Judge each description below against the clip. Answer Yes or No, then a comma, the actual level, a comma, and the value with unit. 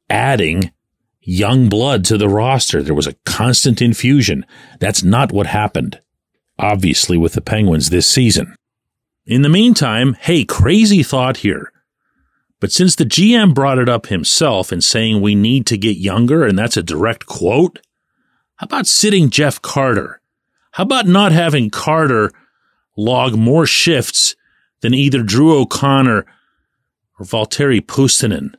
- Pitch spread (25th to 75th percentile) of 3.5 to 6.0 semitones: Yes, average, 5.1 semitones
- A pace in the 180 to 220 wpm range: No, average, 145 wpm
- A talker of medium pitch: No, low, 120 Hz